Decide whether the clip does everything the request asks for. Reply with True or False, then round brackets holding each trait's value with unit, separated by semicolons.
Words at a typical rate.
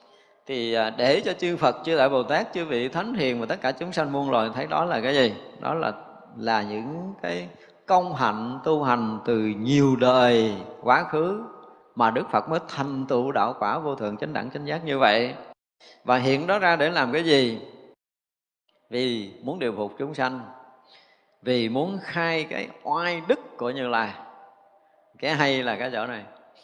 True (190 wpm)